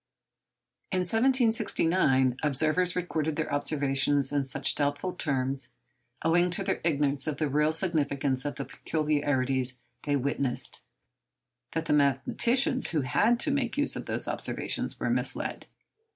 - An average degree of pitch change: Yes, average, 4.5 semitones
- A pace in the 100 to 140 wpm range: Yes, slow, 135 wpm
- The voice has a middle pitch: Yes, medium, 150 Hz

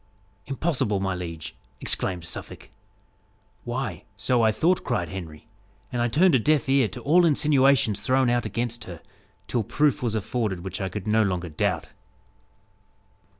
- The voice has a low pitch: Yes, low, 115 Hz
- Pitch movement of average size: No, wide, 5.9 semitones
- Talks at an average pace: Yes, average, 150 wpm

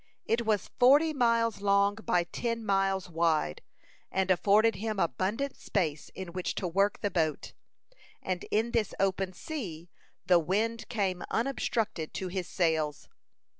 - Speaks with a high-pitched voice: Yes, high, 195 Hz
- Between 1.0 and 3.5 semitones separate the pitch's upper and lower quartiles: No, average, 4.2 semitones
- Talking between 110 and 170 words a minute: Yes, average, 140 wpm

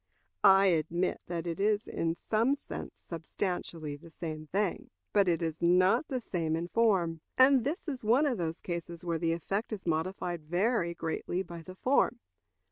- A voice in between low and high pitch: Yes, medium, 175 Hz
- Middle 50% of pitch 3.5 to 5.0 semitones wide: Yes, average, 4.2 semitones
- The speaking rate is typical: Yes, average, 175 wpm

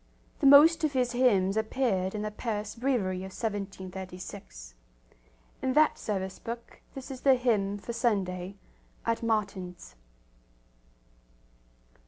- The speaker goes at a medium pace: No, slow, 120 wpm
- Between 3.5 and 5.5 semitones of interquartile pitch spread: Yes, average, 4.7 semitones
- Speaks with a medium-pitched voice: No, high, 210 Hz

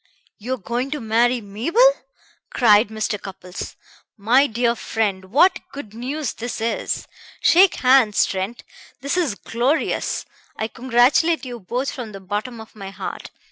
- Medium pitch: No, high, 235 Hz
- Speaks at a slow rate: No, average, 145 wpm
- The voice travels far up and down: No, average, 3.8 semitones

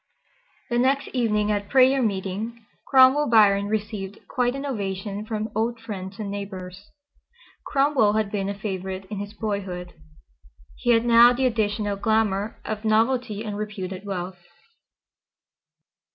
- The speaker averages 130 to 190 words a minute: Yes, slow, 135 wpm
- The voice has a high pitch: Yes, high, 210 Hz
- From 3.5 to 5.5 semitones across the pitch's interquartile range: No, average, 2.8 semitones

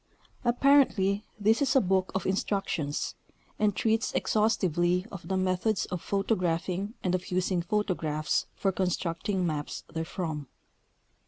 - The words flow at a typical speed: No, slow, 120 wpm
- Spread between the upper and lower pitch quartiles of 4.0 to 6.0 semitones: No, average, 3.2 semitones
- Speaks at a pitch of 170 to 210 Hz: Yes, high, 190 Hz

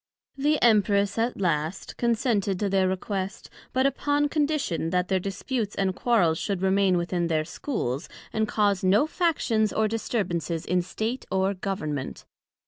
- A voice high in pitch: Yes, high, 200 Hz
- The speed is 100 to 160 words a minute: Yes, average, 145 wpm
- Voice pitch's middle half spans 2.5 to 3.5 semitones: No, average, 4.2 semitones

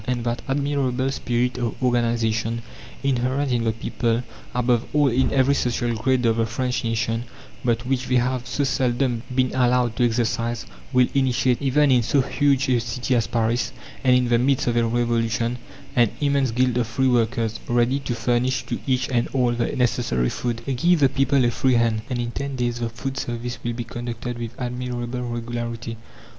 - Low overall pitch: Yes, low, 120 Hz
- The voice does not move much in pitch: Yes, narrow, 1.7 semitones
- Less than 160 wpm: No, average, 185 wpm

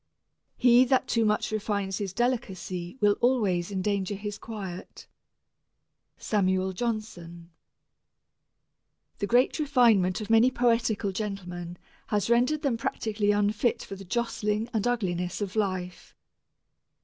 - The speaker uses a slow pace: Yes, slow, 115 wpm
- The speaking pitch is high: Yes, high, 210 Hz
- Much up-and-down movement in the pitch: No, average, 3.6 semitones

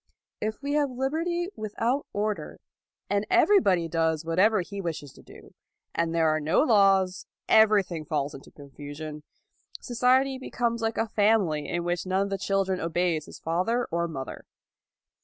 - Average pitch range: No, wide, 5.7 semitones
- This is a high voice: Yes, high, 195 Hz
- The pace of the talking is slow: No, average, 155 wpm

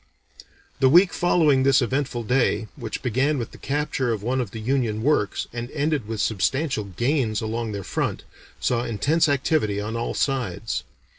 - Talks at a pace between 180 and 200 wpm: No, average, 165 wpm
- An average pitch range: Yes, average, 4.2 semitones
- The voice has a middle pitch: No, low, 125 Hz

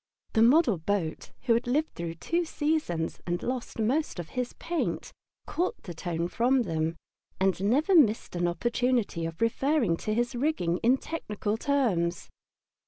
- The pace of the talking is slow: No, average, 155 wpm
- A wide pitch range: Yes, wide, 7.6 semitones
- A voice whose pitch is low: No, high, 230 Hz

